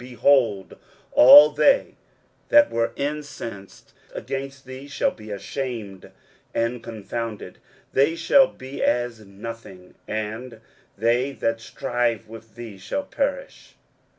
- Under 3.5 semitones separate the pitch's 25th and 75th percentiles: No, average, 3.9 semitones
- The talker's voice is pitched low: Yes, low, 120 Hz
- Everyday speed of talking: No, slow, 115 wpm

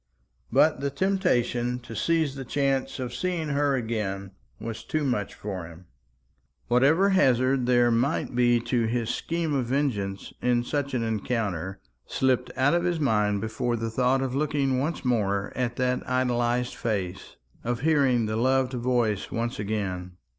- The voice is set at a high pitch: No, low, 125 Hz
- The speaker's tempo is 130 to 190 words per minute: Yes, average, 155 wpm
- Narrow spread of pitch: No, average, 3.5 semitones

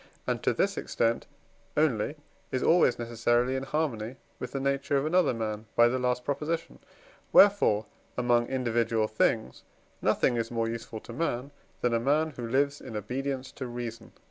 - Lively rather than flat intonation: No, average, 3.1 semitones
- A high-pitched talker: No, low, 125 Hz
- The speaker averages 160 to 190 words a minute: Yes, average, 165 wpm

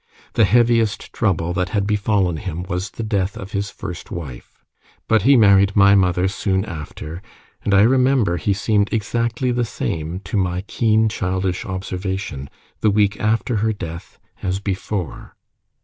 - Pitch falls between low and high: No, low, 100 Hz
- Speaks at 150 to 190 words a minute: Yes, average, 155 wpm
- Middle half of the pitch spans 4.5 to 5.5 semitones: No, average, 3.0 semitones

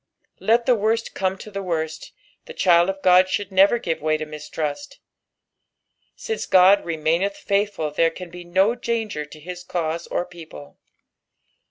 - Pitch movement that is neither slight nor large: Yes, average, 3.9 semitones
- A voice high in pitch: No, medium, 180 Hz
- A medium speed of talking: Yes, average, 160 wpm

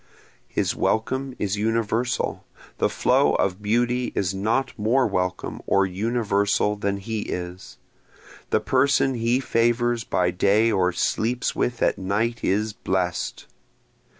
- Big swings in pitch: No, average, 3.5 semitones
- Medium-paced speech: No, slow, 125 wpm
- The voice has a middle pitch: No, low, 110 Hz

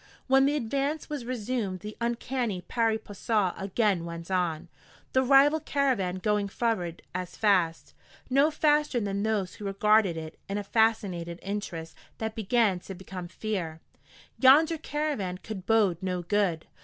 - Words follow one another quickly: No, average, 145 wpm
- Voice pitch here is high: Yes, high, 210 Hz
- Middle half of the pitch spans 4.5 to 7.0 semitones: Yes, average, 5.1 semitones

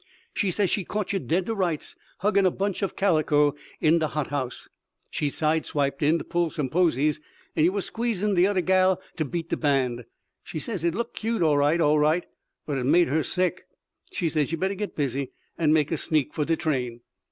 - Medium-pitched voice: Yes, medium, 160 Hz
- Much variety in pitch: No, average, 4.1 semitones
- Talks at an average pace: No, fast, 220 wpm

